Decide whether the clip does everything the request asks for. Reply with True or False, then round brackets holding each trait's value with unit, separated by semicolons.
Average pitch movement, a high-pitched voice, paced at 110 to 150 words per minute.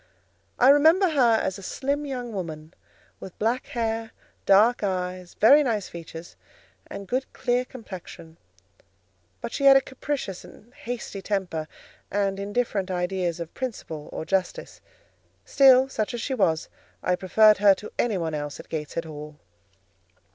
False (5.7 semitones; 205 Hz; 145 wpm)